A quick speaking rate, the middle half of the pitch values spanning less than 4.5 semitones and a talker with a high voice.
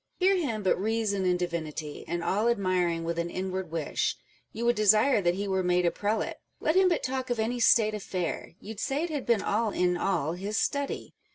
No: fast, 210 wpm; average, 4.8 semitones; high, 200 Hz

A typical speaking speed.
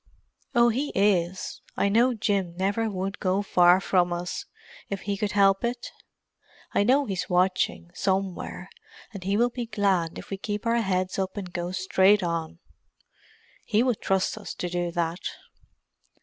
Yes: average, 165 wpm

